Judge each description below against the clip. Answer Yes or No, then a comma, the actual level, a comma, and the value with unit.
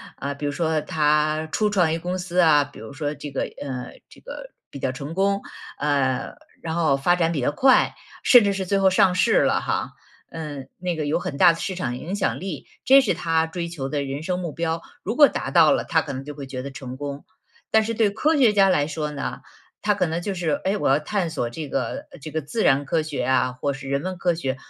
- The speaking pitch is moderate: Yes, medium, 160 Hz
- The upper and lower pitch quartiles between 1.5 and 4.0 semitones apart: No, average, 4.7 semitones